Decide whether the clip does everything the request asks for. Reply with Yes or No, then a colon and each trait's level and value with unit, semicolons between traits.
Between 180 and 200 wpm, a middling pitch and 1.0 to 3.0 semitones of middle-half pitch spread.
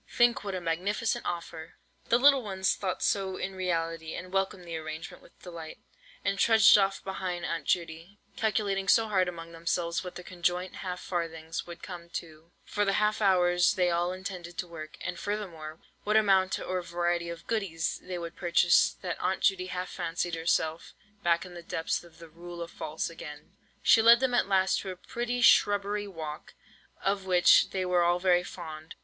Yes: average, 185 wpm; medium, 180 Hz; narrow, 2.6 semitones